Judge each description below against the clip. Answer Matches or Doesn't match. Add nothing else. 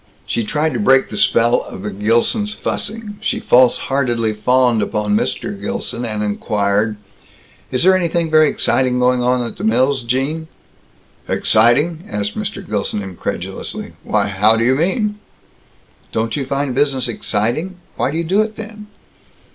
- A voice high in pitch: Doesn't match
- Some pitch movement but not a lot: Doesn't match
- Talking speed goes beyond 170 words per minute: Doesn't match